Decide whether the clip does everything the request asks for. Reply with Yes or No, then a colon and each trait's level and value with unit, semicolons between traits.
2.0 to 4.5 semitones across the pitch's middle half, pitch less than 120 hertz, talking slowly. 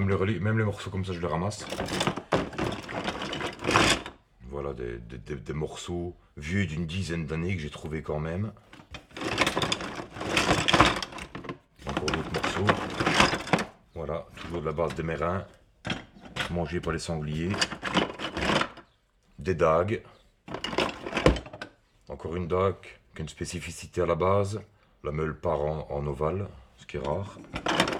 Yes: average, 3.3 semitones; very low, 85 Hz; slow, 120 wpm